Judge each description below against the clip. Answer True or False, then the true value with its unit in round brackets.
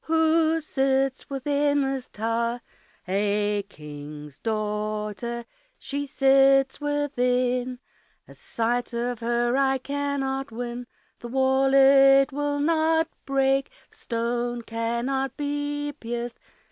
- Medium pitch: False (265 Hz)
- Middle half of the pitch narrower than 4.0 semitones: True (3.0 semitones)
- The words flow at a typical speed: False (105 wpm)